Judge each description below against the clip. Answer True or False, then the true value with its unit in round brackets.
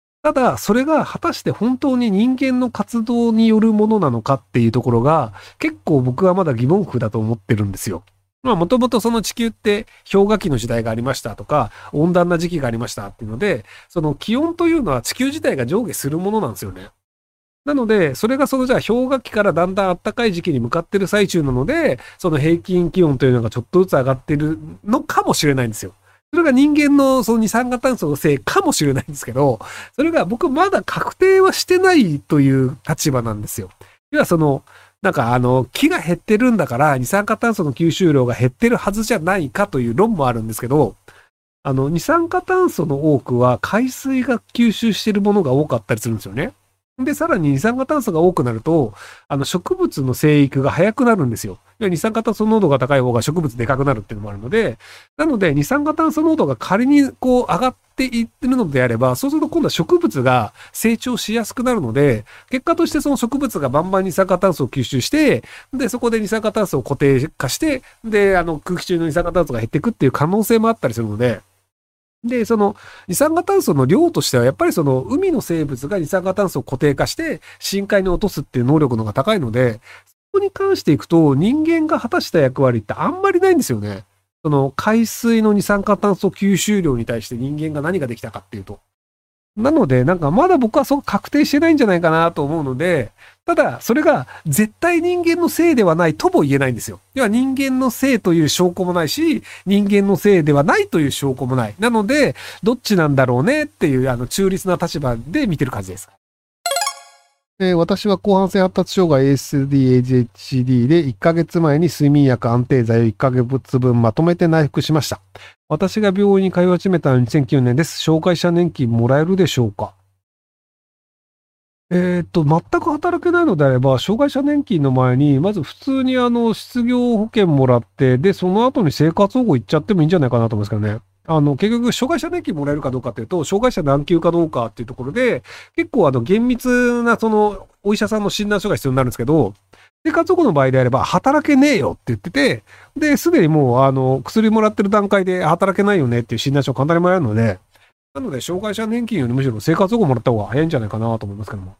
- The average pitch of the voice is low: False (175 Hz)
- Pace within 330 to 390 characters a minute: False (415 characters per minute)